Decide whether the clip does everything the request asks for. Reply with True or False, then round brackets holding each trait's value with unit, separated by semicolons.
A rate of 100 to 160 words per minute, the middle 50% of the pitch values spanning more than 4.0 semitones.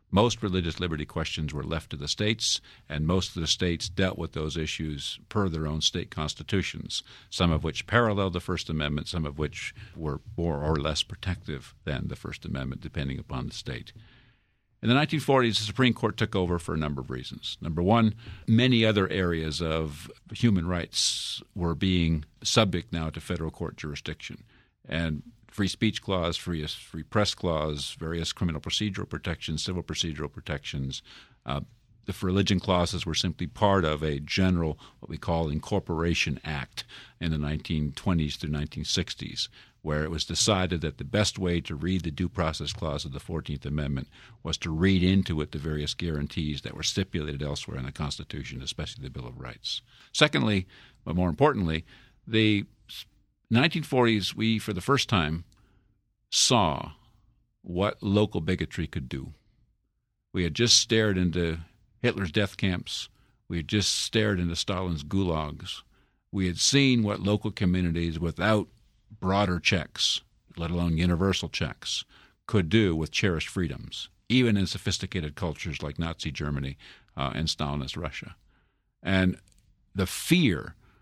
True (155 wpm; 4.9 semitones)